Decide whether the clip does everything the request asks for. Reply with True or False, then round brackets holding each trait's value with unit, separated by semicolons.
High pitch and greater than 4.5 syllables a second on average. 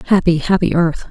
False (170 Hz; 5.6 syllables/s)